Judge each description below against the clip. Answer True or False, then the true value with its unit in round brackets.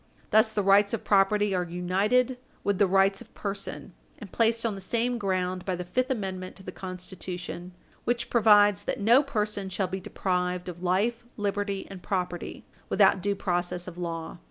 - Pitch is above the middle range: True (195 Hz)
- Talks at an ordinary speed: True (180 wpm)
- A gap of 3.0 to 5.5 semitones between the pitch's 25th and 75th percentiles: False (2.6 semitones)